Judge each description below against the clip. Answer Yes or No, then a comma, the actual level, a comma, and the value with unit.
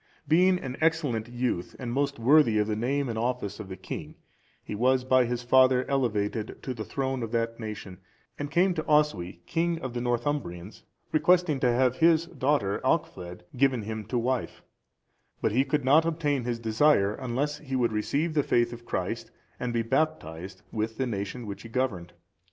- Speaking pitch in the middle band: No, low, 125 Hz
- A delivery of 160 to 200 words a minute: Yes, average, 185 wpm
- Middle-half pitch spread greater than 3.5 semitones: Yes, average, 4.5 semitones